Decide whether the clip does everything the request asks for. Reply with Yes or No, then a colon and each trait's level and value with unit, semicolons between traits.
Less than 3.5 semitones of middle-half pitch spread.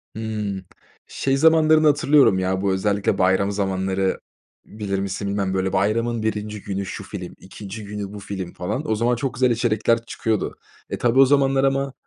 No: average, 4.0 semitones